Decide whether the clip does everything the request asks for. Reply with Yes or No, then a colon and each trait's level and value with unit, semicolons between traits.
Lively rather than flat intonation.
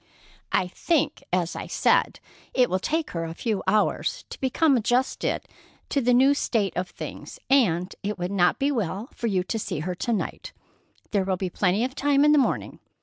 Yes: wide, 6.2 semitones